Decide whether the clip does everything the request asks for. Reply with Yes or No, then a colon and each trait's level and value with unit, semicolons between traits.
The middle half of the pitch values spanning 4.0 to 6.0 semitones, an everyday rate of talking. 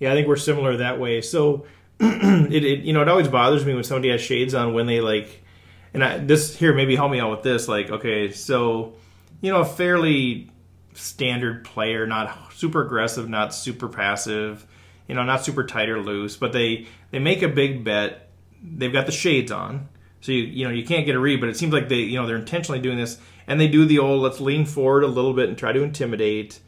No: average, 4.6 semitones; fast, 230 wpm